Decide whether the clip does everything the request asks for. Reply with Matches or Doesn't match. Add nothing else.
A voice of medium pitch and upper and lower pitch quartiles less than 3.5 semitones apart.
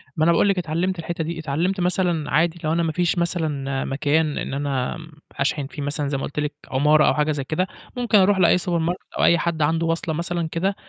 Matches